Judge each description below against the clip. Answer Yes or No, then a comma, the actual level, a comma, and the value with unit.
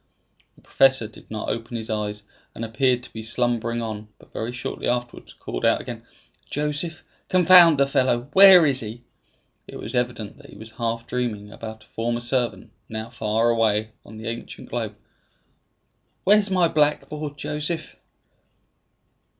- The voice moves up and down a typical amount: Yes, average, 3.9 semitones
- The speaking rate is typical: Yes, average, 155 wpm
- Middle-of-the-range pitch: No, low, 120 Hz